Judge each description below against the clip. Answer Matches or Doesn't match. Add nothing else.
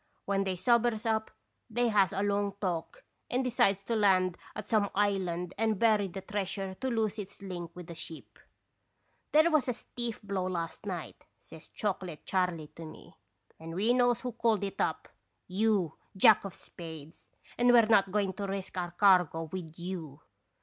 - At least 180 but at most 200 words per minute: Matches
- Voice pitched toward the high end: Matches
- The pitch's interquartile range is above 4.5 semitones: Doesn't match